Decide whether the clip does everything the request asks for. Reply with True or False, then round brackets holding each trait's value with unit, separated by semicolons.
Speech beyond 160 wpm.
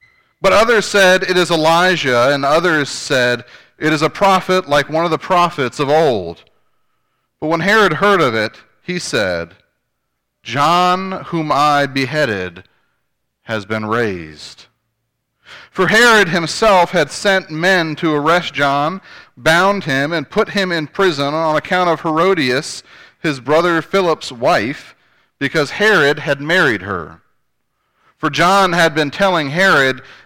False (140 wpm)